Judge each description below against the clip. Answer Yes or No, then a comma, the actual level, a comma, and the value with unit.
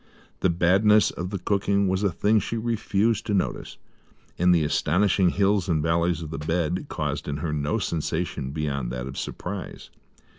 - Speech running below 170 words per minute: No, average, 175 wpm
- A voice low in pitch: Yes, very low, 90 Hz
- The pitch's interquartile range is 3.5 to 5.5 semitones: Yes, average, 4.6 semitones